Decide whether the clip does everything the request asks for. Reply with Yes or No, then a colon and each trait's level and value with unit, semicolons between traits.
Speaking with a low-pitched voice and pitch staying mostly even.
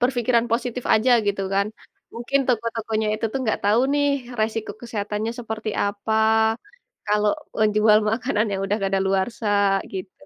No: high, 220 Hz; narrow, 2.1 semitones